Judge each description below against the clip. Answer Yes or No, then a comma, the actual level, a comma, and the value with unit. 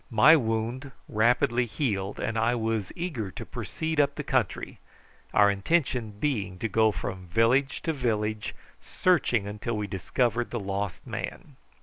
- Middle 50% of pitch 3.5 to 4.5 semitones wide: Yes, average, 3.9 semitones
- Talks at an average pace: Yes, average, 145 wpm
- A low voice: Yes, low, 115 Hz